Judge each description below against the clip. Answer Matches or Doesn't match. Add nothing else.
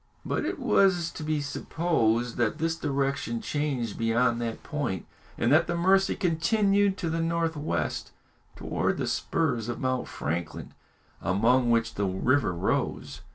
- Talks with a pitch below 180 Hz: Matches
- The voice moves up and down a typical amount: Doesn't match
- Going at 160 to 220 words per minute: Doesn't match